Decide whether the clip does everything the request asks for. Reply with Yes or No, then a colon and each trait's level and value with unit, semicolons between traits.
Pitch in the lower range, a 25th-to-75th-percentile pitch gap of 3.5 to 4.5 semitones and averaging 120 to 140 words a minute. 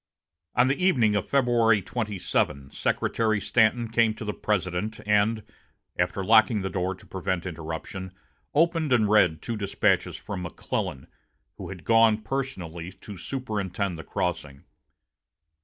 Yes: low, 105 Hz; average, 3.9 semitones; slow, 135 wpm